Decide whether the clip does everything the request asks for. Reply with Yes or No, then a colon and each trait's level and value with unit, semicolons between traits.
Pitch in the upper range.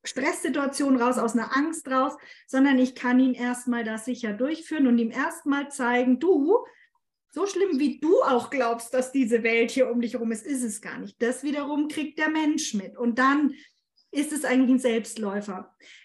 Yes: very high, 260 Hz